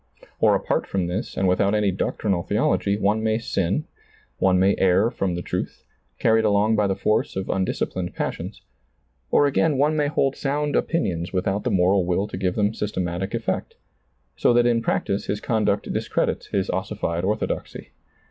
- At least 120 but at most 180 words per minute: Yes, average, 175 wpm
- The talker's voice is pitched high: No, low, 100 Hz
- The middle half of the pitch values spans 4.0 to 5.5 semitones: No, average, 3.1 semitones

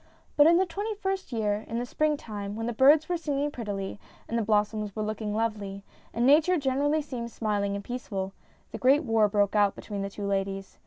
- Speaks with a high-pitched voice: Yes, high, 225 Hz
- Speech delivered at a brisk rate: Yes, fast, 210 wpm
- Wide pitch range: Yes, wide, 6.0 semitones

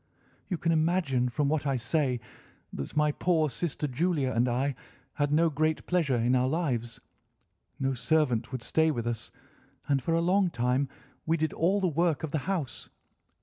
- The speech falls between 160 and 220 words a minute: Yes, average, 180 wpm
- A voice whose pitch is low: No, medium, 150 Hz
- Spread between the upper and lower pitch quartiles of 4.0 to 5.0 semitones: Yes, average, 4.5 semitones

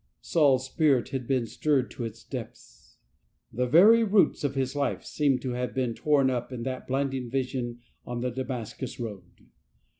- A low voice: Yes, low, 130 Hz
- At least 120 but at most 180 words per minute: Yes, average, 175 wpm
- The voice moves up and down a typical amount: No, narrow, 2.3 semitones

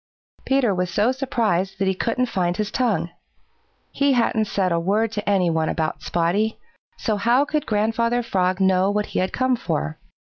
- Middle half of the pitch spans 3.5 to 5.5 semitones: Yes, average, 4.3 semitones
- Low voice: No, high, 205 Hz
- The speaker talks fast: No, average, 180 wpm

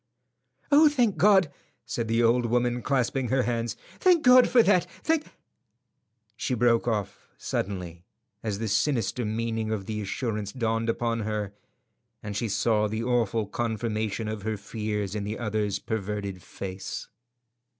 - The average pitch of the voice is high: No, low, 115 Hz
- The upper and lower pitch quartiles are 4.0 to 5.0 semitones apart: No, narrow, 2.6 semitones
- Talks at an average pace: Yes, average, 145 wpm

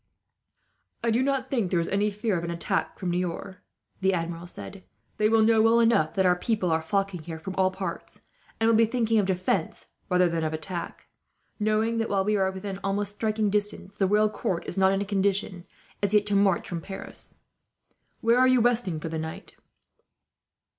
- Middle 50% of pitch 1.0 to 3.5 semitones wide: Yes, average, 3.2 semitones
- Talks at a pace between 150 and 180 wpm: No, average, 200 wpm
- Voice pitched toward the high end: Yes, high, 195 Hz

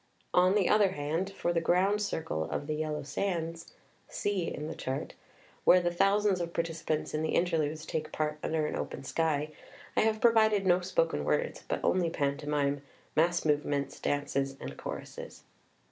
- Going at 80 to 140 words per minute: No, average, 170 wpm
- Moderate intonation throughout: Yes, average, 3.7 semitones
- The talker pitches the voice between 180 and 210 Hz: No, medium, 165 Hz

